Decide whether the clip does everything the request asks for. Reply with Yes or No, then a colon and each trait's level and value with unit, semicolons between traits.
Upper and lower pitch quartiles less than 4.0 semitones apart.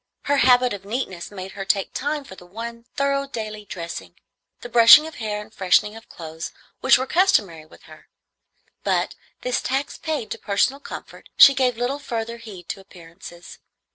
No: average, 5.2 semitones